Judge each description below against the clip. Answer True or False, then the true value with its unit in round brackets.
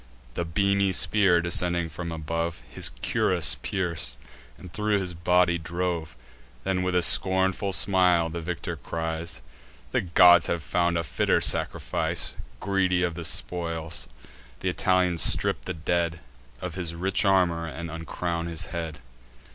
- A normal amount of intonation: False (1.7 semitones)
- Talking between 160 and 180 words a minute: False (140 wpm)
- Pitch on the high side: False (85 Hz)